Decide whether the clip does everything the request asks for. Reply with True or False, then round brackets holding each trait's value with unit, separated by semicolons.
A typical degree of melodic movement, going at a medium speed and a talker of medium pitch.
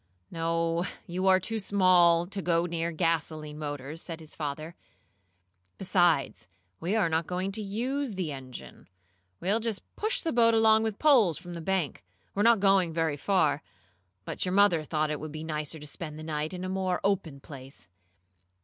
True (4.0 semitones; 175 wpm; 170 Hz)